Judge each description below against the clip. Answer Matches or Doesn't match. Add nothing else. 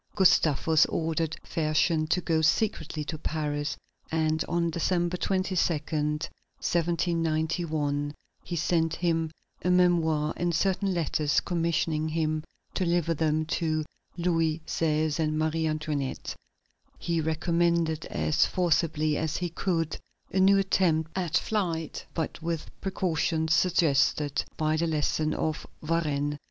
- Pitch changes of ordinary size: Doesn't match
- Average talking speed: Doesn't match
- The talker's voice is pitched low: Doesn't match